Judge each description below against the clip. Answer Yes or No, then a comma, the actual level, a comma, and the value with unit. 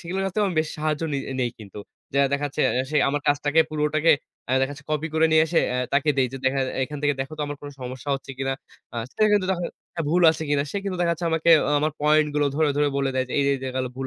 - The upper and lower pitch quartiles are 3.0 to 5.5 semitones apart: No, narrow, 2.6 semitones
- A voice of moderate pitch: Yes, medium, 145 Hz